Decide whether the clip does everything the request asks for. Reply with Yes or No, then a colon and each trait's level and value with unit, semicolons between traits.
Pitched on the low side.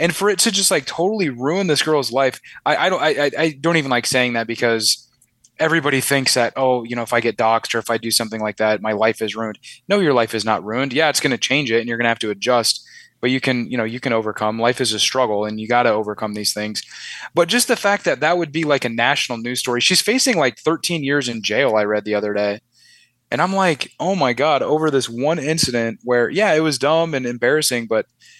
Yes: low, 120 Hz